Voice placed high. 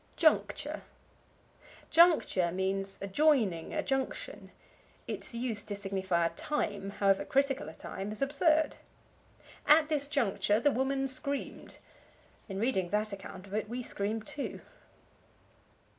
Yes: high, 220 Hz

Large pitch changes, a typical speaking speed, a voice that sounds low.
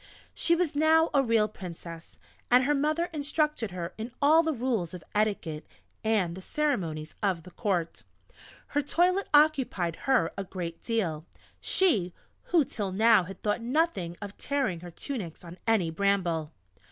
No: wide, 8.5 semitones; average, 155 wpm; high, 215 Hz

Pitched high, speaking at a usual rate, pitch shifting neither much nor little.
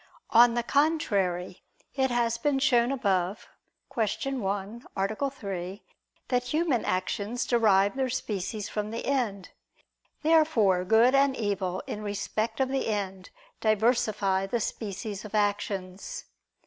No: high, 220 Hz; slow, 125 wpm; average, 4.1 semitones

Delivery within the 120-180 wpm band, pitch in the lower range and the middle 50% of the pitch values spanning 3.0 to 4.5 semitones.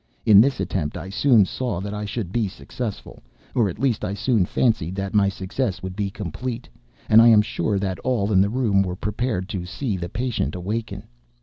No: average, 195 wpm; low, 105 Hz; average, 3.6 semitones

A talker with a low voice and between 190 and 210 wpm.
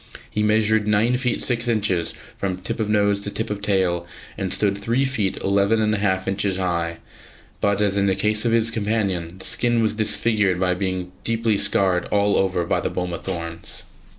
Yes: low, 100 Hz; average, 195 wpm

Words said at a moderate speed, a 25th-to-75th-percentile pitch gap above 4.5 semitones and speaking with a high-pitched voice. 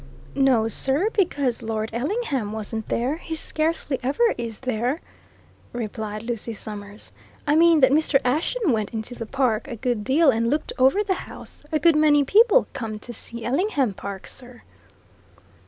Yes: average, 160 wpm; wide, 5.5 semitones; very high, 255 Hz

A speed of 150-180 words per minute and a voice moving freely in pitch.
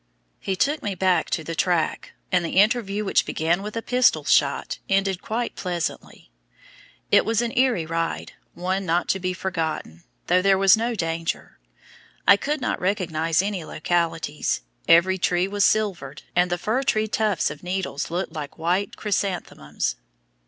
No: average, 160 wpm; average, 3.6 semitones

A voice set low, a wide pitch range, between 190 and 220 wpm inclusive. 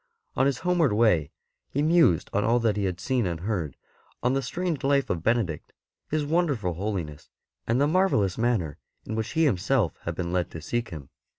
Yes: low, 110 Hz; wide, 7.6 semitones; average, 195 wpm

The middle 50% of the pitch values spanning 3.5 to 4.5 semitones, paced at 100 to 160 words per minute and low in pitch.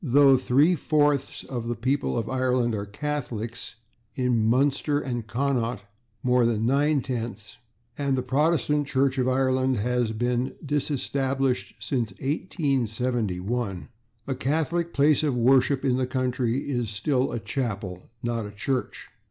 No: average, 2.9 semitones; average, 140 wpm; low, 130 Hz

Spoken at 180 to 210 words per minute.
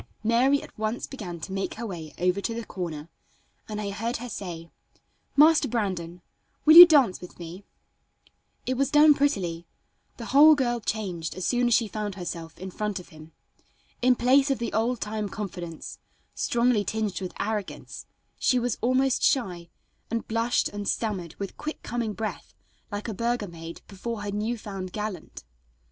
No: average, 170 wpm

